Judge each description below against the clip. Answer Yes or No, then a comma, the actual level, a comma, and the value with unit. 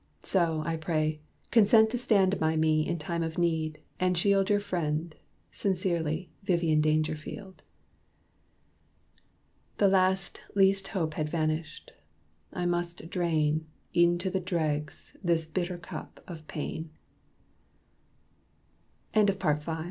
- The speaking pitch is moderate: Yes, medium, 170 Hz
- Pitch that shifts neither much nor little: Yes, average, 3.2 semitones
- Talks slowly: Yes, slow, 120 wpm